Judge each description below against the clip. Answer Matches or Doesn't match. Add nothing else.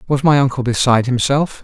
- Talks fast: Doesn't match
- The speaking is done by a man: Matches